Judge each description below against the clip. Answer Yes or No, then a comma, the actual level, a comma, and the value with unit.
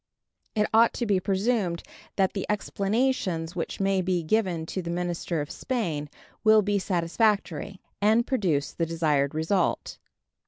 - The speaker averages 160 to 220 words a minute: No, average, 145 wpm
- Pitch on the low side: No, high, 190 Hz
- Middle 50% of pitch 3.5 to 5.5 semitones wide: Yes, average, 4.0 semitones